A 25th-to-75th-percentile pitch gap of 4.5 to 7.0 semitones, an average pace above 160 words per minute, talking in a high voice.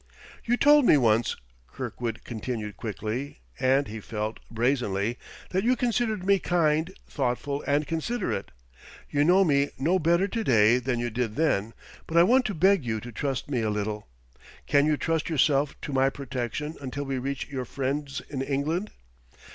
No: wide, 5.4 semitones; average, 170 wpm; medium, 140 Hz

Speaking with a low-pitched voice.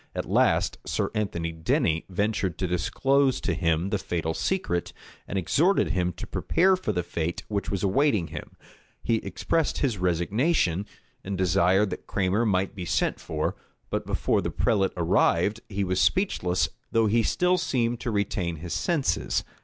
Yes: low, 100 Hz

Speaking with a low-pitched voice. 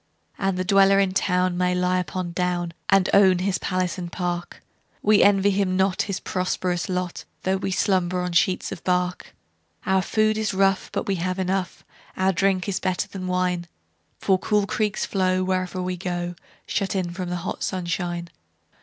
No: medium, 185 Hz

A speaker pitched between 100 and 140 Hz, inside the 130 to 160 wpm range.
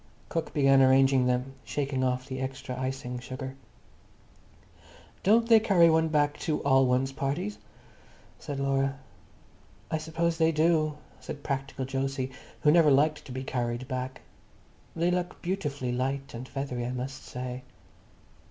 Yes: low, 135 Hz; average, 145 wpm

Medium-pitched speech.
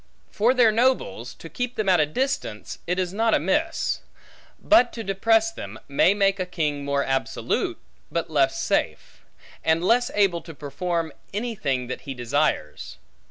Yes: medium, 180 Hz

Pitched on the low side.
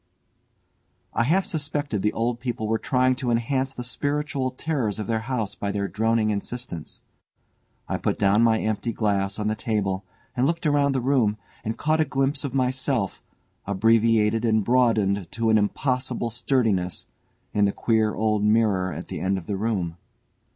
Yes: low, 115 Hz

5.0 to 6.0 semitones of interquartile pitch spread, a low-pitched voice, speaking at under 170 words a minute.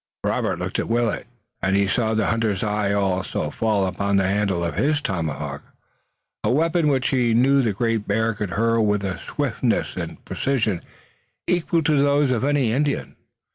No: average, 5.3 semitones; low, 110 Hz; average, 175 wpm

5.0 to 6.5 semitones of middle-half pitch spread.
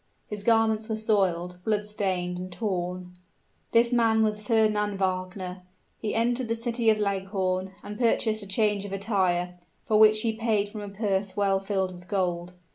No: average, 2.8 semitones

